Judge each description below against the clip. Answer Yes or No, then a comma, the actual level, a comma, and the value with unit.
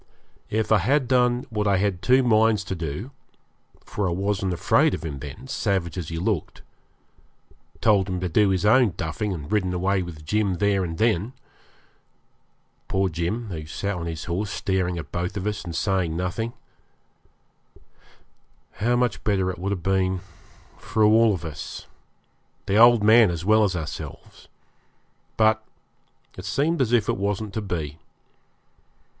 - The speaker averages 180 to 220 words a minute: No, average, 160 wpm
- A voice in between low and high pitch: No, very low, 95 Hz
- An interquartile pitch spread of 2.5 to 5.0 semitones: Yes, average, 3.6 semitones